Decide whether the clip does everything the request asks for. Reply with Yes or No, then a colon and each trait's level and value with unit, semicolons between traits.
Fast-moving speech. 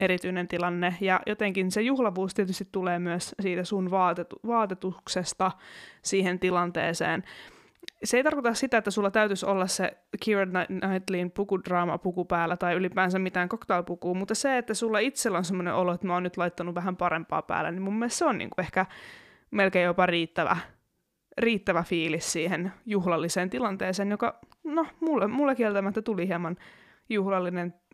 Yes: fast, 160 wpm